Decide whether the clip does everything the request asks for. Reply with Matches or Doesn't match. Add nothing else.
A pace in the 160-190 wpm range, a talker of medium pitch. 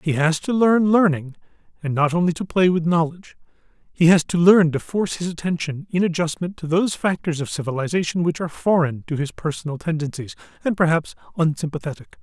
Matches